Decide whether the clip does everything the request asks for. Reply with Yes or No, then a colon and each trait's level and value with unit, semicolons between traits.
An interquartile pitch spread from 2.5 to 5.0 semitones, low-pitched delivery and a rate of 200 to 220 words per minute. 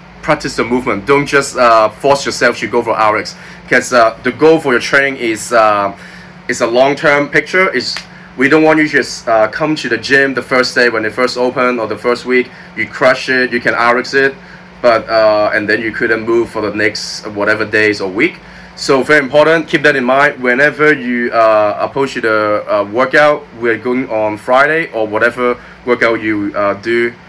Yes: average, 4.6 semitones; low, 125 Hz; fast, 205 wpm